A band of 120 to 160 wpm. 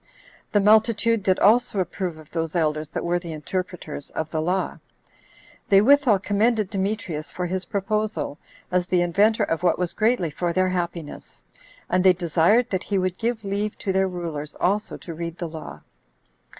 No: average, 175 wpm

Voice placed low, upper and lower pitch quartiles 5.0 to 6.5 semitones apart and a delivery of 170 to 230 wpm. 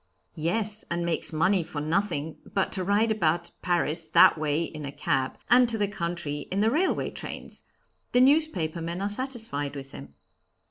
No: medium, 175 Hz; average, 5.3 semitones; average, 175 wpm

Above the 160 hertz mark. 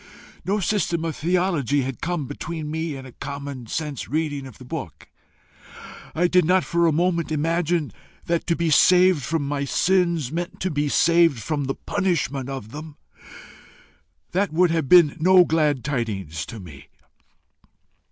No: medium, 155 Hz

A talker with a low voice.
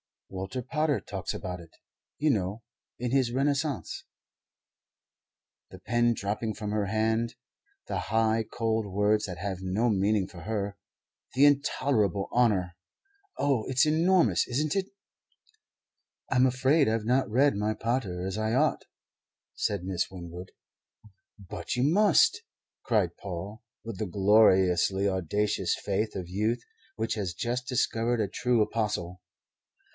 Yes: low, 110 Hz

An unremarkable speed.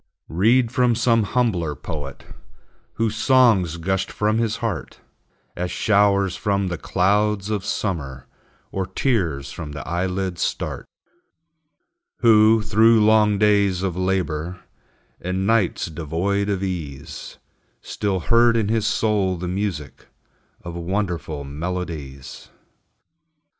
No: slow, 115 wpm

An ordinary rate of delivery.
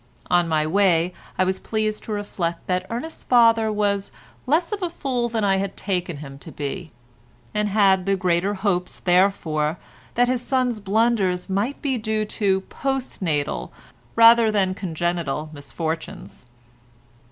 Yes: average, 145 wpm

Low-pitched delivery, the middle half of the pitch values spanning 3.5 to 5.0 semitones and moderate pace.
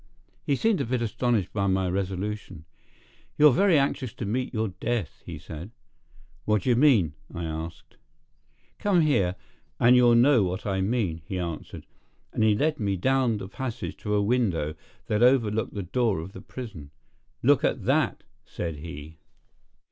No: low, 105 Hz; wide, 5.5 semitones; average, 165 wpm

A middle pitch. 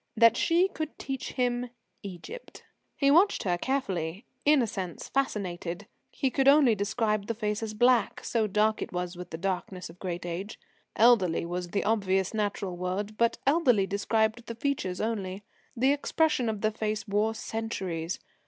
No: high, 215 Hz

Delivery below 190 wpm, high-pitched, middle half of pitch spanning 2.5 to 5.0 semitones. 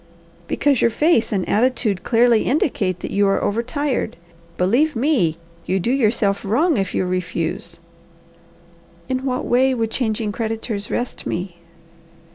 Yes: average, 140 wpm; high, 225 Hz; average, 4.6 semitones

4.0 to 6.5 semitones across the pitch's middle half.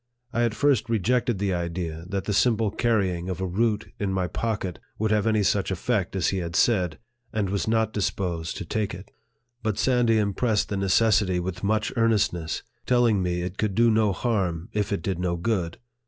No: average, 3.5 semitones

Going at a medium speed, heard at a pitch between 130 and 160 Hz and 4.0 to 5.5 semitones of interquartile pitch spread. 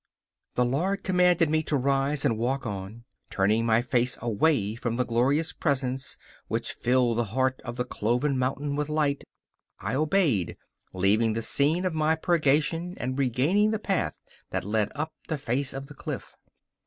Yes: average, 170 wpm; low, 135 Hz; average, 4.6 semitones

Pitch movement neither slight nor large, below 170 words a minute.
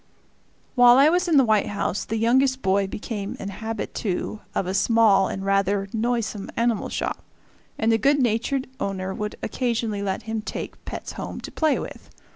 No: average, 3.5 semitones; average, 175 wpm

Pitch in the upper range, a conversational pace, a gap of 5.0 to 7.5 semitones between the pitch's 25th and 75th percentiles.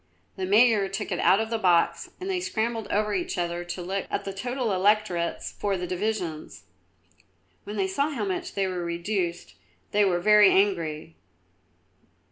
No: high, 195 Hz; average, 170 wpm; average, 3.4 semitones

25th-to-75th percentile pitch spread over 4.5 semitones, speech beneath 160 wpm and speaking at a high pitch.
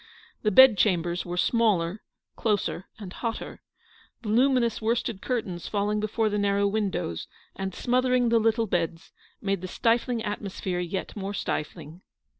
No: average, 3.6 semitones; slow, 135 wpm; high, 205 Hz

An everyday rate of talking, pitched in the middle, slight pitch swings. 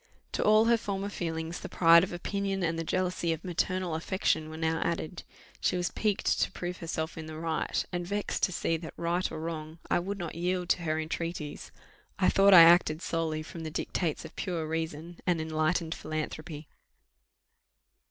Yes: average, 185 wpm; medium, 170 Hz; narrow, 2.2 semitones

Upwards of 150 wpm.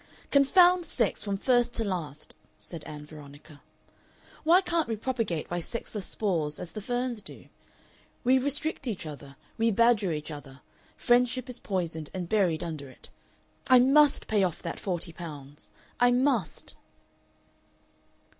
No: average, 145 wpm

